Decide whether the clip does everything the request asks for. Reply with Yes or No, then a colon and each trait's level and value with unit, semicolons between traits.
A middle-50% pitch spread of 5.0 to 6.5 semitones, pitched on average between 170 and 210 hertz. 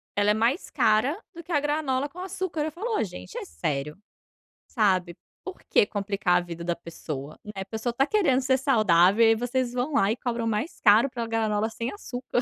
No: wide, 5.6 semitones; high, 230 Hz